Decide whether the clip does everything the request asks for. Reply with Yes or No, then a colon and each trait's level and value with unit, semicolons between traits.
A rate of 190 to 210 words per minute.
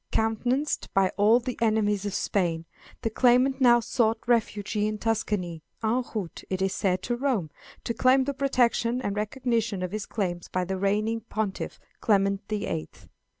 No: average, 165 wpm